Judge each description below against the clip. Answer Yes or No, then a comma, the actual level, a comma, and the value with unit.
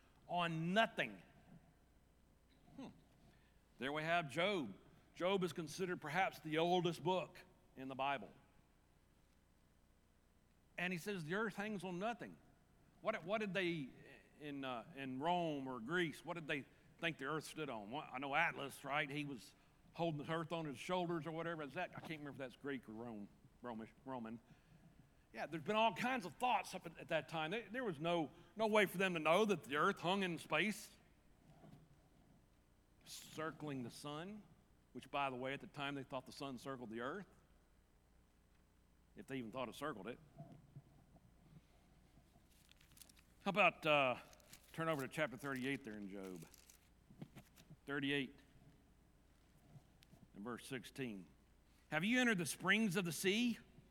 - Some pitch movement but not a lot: No, wide, 6.5 semitones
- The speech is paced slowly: No, average, 160 wpm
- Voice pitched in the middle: Yes, medium, 150 Hz